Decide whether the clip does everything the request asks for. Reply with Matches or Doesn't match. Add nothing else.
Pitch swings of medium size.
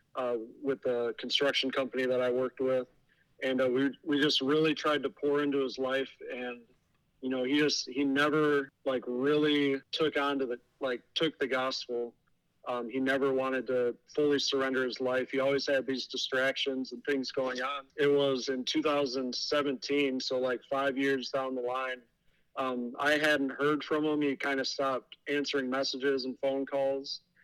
Doesn't match